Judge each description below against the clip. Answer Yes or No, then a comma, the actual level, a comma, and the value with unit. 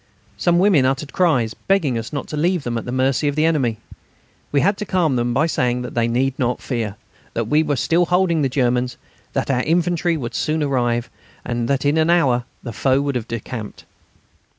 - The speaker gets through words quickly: Yes, fast, 210 wpm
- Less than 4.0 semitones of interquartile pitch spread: No, average, 4.7 semitones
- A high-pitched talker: No, low, 135 Hz